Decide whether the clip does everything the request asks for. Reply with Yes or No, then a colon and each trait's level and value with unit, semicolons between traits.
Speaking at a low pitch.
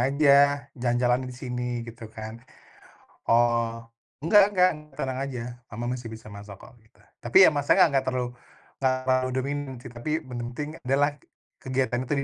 Yes: low, 125 Hz